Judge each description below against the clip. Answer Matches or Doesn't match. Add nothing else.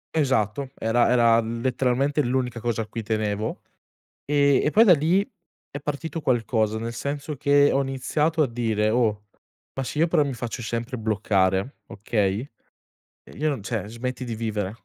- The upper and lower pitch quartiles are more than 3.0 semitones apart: Matches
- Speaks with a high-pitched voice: Doesn't match